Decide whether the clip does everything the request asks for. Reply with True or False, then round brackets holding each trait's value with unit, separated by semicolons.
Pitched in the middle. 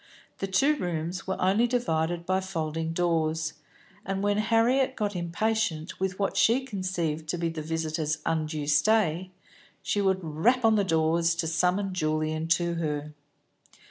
True (175 Hz)